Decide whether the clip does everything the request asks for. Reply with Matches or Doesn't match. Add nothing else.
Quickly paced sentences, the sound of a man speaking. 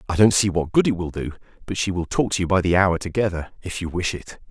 Matches